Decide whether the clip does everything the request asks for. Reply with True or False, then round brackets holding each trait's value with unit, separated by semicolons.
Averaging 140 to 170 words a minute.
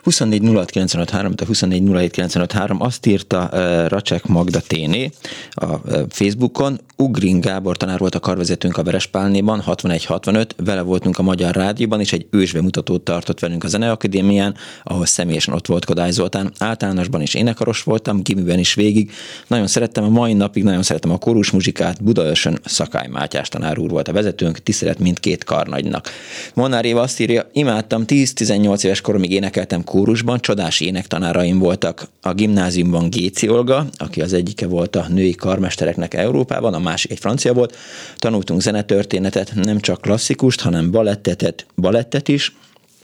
True (150 wpm)